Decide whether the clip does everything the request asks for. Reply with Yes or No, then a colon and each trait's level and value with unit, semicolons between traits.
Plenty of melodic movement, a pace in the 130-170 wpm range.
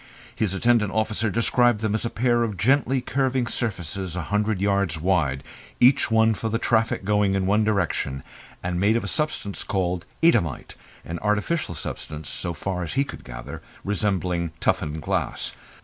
No: average, 4.4 semitones; average, 165 wpm